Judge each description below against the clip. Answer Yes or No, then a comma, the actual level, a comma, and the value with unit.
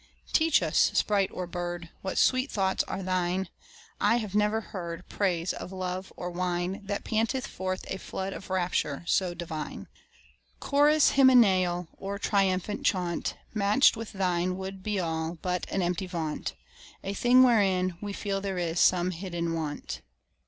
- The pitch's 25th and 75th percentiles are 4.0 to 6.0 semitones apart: No, narrow, 2.4 semitones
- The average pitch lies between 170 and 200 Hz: Yes, medium, 185 Hz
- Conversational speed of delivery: Yes, average, 155 wpm